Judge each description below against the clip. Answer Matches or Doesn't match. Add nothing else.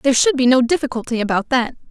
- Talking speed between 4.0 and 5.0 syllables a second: Doesn't match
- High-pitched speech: Matches